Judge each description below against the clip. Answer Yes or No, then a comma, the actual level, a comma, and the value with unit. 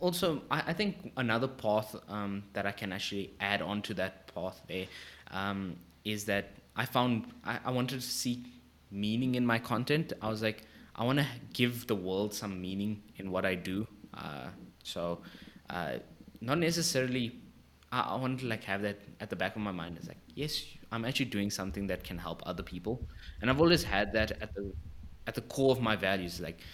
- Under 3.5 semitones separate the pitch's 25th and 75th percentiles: No, average, 4.5 semitones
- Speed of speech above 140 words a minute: Yes, average, 200 wpm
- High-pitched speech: No, low, 105 Hz